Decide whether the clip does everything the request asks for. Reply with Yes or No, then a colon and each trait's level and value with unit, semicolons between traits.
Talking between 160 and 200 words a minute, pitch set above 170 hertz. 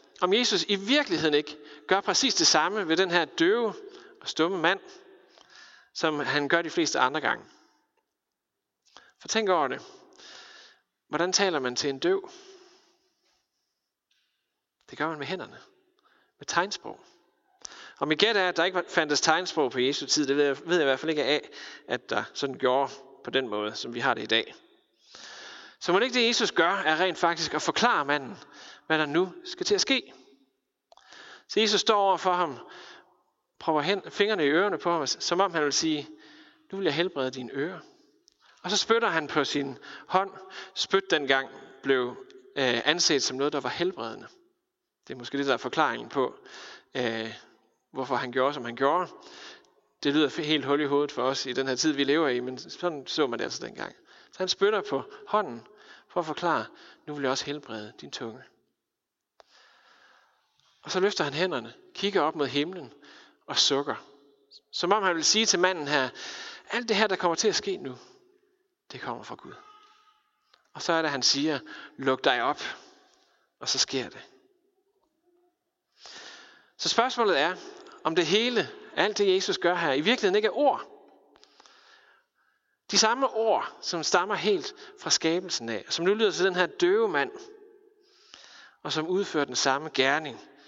Yes: average, 180 wpm; high, 190 Hz